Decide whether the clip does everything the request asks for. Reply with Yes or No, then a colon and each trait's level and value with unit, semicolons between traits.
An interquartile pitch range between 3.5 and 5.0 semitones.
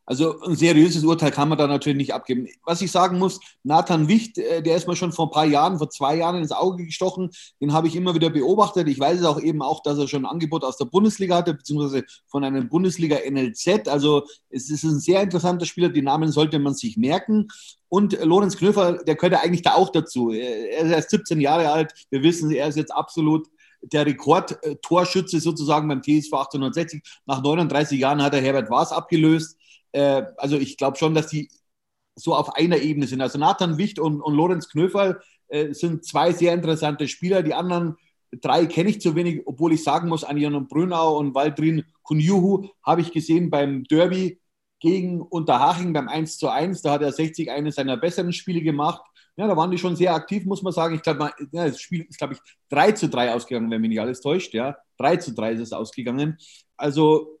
No: average, 3.0 semitones